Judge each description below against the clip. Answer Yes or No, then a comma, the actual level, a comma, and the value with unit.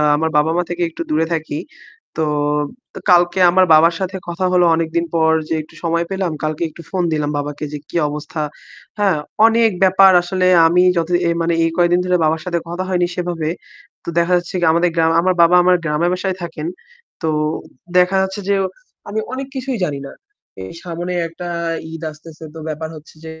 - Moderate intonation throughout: No, narrow, 2.2 semitones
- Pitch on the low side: No, medium, 170 Hz